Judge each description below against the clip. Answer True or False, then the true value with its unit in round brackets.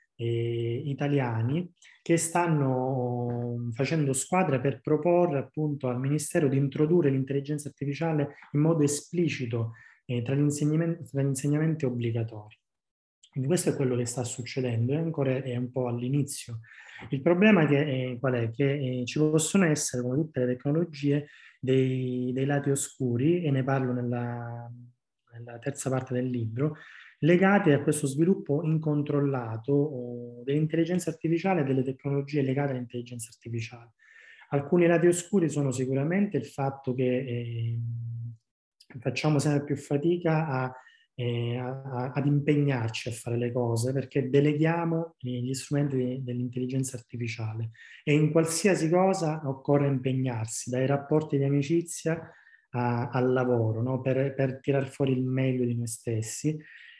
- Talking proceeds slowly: False (135 wpm)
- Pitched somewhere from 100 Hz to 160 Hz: True (135 Hz)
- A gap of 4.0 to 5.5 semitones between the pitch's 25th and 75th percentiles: False (3.4 semitones)